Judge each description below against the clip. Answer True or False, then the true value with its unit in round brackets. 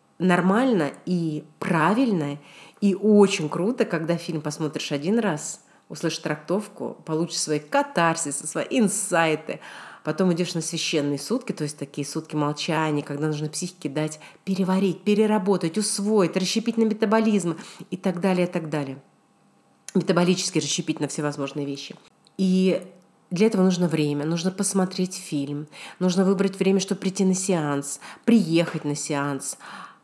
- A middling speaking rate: True (135 wpm)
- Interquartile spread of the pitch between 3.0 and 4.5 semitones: True (4.2 semitones)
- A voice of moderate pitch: True (175 Hz)